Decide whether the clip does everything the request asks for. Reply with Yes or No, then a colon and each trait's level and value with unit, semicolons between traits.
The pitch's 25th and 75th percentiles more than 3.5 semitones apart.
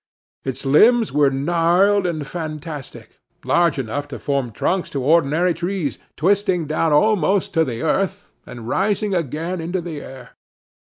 Yes: average, 4.5 semitones